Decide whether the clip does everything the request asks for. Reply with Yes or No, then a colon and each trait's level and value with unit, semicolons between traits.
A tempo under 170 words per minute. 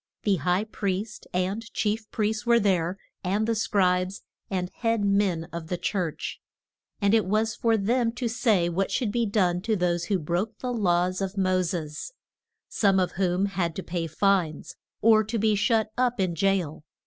No: average, 180 wpm